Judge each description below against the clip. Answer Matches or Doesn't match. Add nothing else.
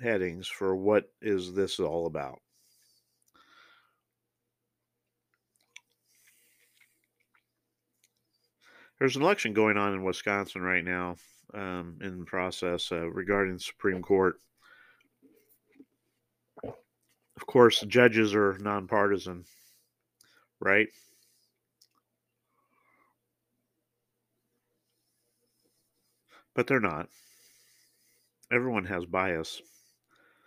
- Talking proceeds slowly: Matches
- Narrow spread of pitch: Doesn't match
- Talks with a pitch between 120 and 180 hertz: Doesn't match